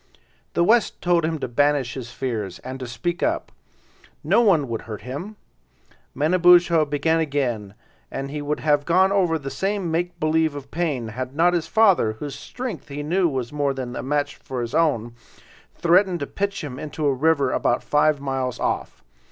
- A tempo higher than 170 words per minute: Yes, average, 185 wpm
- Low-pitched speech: No, medium, 150 Hz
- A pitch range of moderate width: Yes, average, 4.7 semitones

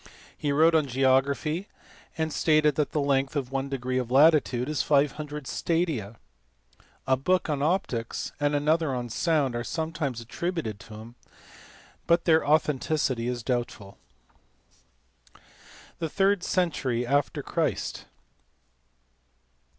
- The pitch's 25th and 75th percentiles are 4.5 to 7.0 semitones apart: No, average, 3.9 semitones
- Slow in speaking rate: Yes, slow, 120 wpm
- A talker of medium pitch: Yes, medium, 145 Hz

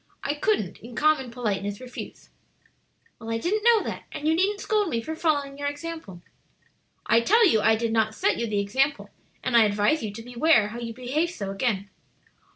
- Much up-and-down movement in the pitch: Yes, wide, 6.4 semitones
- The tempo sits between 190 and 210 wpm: Yes, average, 195 wpm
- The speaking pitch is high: Yes, high, 245 Hz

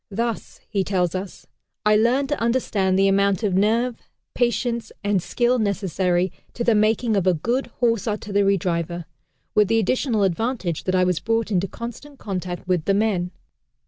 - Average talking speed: Yes, average, 170 wpm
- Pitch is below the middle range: No, high, 205 Hz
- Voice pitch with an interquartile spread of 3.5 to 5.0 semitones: Yes, average, 3.8 semitones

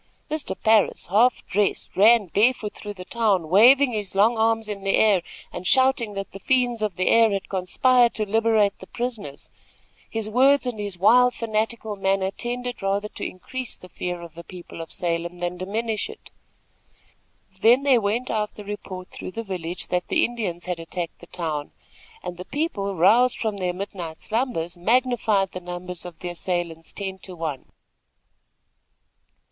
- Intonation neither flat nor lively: Yes, average, 4.2 semitones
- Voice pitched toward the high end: Yes, high, 205 Hz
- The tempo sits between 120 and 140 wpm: No, average, 170 wpm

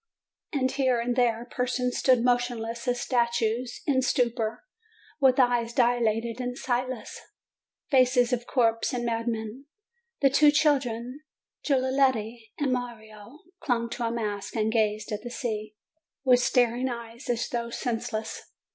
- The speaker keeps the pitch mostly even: Yes, narrow, 1.8 semitones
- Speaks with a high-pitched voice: Yes, high, 240 Hz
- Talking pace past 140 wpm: No, slow, 135 wpm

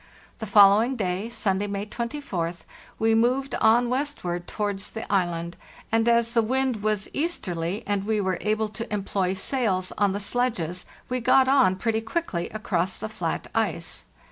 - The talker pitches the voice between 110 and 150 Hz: No, high, 215 Hz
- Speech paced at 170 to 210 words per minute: No, average, 160 wpm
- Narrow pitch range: No, average, 3.8 semitones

